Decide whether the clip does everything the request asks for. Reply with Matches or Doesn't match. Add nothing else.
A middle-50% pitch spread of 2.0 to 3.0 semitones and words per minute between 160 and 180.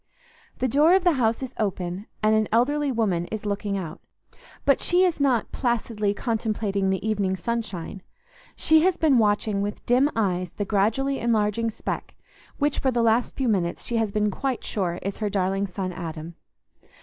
Doesn't match